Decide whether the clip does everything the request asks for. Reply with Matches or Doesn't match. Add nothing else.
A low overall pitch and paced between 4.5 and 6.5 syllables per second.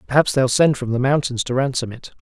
Matches